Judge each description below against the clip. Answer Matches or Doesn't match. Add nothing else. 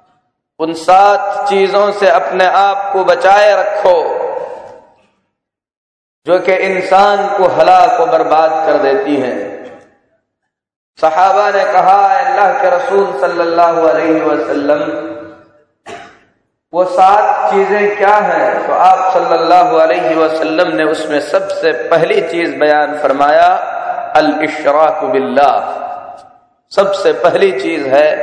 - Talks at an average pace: Doesn't match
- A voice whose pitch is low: Doesn't match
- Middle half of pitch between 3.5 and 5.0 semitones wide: Matches